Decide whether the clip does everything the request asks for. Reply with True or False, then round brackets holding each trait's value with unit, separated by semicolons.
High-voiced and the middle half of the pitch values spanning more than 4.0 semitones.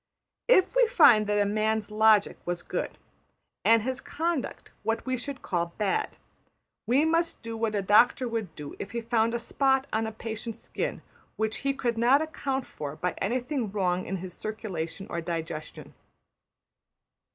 True (220 Hz; 4.4 semitones)